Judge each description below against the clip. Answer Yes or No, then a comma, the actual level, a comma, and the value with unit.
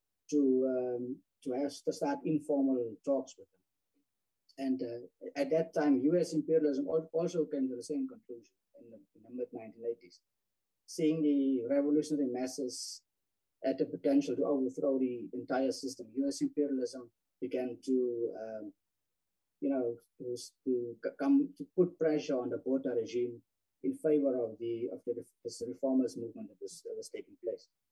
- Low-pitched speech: Yes, low, 130 Hz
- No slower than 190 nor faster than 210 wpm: No, average, 155 wpm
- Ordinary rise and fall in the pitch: Yes, average, 4.4 semitones